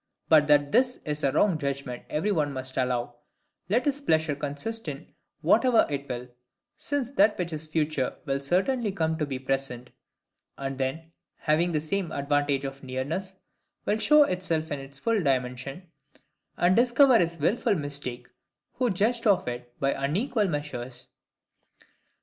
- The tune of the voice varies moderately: No, wide, 6.4 semitones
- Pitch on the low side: No, medium, 150 Hz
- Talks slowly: No, average, 155 wpm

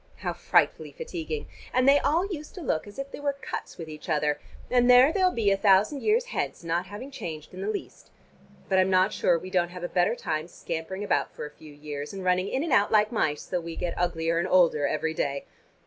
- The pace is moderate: No, fast, 235 wpm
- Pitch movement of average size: No, wide, 7.9 semitones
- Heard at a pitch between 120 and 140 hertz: No, high, 190 Hz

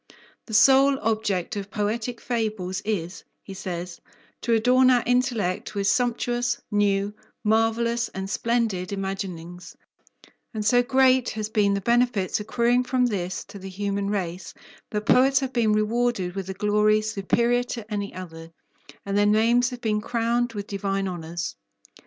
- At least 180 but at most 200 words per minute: No, average, 150 wpm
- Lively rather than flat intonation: No, average, 3.5 semitones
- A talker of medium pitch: No, high, 210 Hz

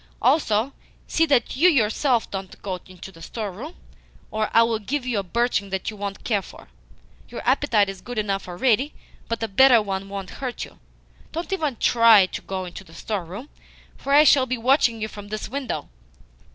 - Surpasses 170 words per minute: Yes, average, 190 wpm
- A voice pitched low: No, high, 220 Hz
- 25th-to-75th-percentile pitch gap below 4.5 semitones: No, average, 4.8 semitones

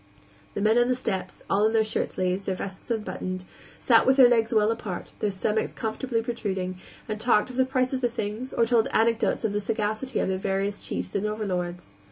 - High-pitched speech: Yes, high, 215 Hz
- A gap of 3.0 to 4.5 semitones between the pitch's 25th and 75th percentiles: Yes, average, 3.4 semitones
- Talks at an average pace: No, fast, 210 wpm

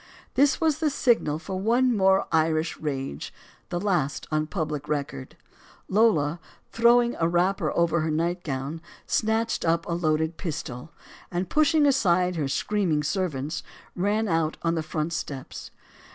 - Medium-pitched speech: Yes, medium, 170 Hz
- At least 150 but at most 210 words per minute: No, average, 140 wpm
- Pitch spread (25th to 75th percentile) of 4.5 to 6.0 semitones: Yes, average, 5.1 semitones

